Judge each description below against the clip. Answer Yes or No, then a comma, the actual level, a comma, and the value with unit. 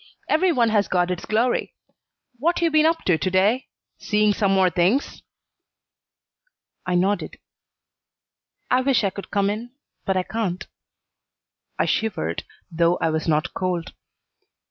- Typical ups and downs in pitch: Yes, average, 5.0 semitones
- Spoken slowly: No, average, 145 wpm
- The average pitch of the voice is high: Yes, high, 200 Hz